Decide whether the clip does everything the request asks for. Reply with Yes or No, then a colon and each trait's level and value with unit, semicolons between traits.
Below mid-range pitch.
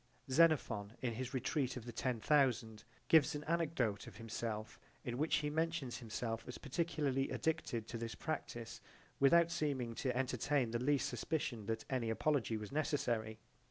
Yes: low, 125 Hz